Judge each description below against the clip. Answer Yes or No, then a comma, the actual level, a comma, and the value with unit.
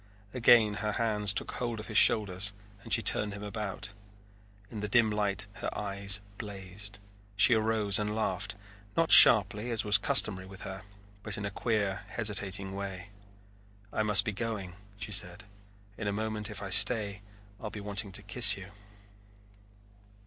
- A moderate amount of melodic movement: No, narrow, 1.6 semitones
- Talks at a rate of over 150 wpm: Yes, average, 165 wpm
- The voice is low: Yes, low, 105 Hz